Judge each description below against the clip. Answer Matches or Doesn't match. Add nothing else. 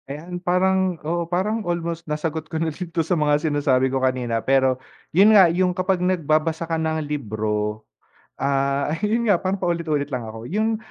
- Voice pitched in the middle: Matches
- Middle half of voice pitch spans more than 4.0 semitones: Matches